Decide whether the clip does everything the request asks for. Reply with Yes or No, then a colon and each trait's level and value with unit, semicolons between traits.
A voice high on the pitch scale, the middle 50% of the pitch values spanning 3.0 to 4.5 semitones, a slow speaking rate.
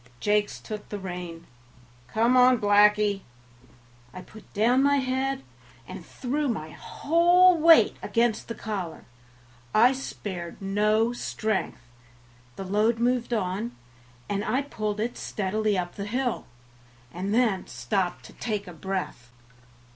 Yes: high, 215 Hz; average, 4.2 semitones; slow, 125 wpm